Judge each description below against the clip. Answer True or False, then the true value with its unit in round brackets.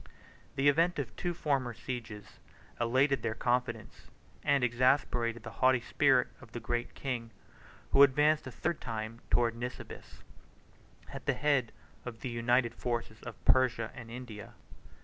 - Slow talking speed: False (150 wpm)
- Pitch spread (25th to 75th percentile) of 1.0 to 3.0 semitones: True (2.5 semitones)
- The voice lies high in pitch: False (125 Hz)